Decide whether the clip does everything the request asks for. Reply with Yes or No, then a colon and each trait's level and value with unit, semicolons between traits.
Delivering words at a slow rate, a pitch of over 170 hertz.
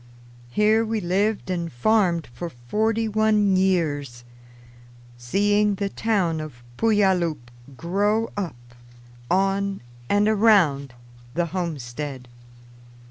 Yes: slow, 95 wpm; medium, 185 Hz